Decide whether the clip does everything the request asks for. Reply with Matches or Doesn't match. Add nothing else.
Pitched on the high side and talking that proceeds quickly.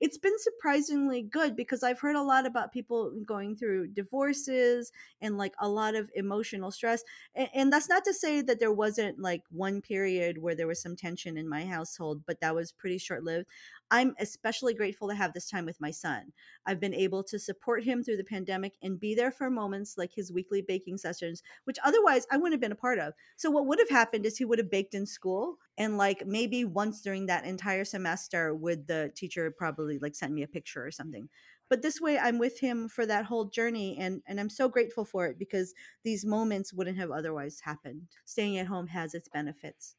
Matches